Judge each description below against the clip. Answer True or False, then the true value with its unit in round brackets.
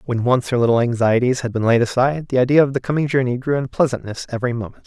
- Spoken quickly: True (245 wpm)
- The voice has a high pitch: False (125 Hz)